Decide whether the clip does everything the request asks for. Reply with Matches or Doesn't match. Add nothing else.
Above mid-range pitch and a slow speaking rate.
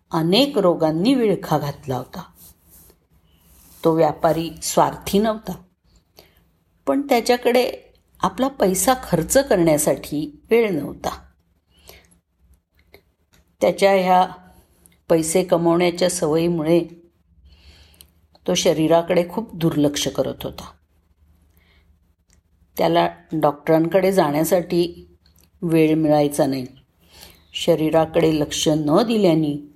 Doesn't match